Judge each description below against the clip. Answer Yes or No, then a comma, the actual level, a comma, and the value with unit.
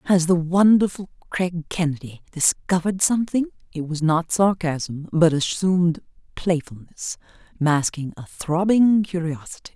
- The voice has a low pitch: No, medium, 170 Hz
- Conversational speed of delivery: No, slow, 110 wpm